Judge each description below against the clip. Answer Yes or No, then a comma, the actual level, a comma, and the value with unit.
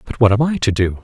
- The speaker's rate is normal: No, fast, 350 wpm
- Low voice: Yes, low, 115 Hz